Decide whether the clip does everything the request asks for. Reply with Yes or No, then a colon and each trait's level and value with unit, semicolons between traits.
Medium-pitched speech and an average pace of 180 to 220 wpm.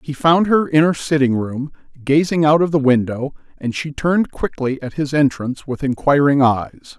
Yes: medium, 145 Hz; average, 190 wpm